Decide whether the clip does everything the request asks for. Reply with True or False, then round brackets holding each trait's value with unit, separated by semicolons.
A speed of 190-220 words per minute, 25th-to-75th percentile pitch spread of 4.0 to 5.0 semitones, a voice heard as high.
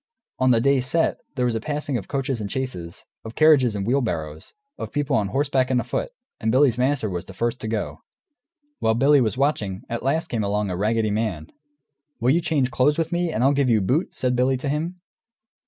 False (205 wpm; 4.5 semitones; 125 Hz)